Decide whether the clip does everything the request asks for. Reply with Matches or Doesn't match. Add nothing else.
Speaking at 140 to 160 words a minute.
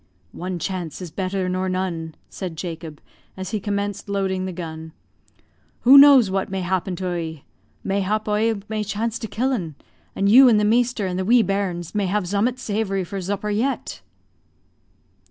Doesn't match